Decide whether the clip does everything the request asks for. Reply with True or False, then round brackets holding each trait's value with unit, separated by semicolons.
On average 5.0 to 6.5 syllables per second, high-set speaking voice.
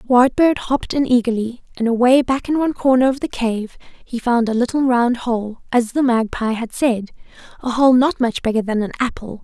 True (5.4 syllables/s; 245 Hz)